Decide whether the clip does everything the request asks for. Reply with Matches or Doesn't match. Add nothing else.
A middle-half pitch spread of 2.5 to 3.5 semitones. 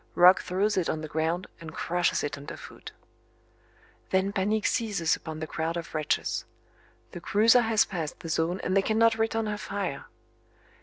Doesn't match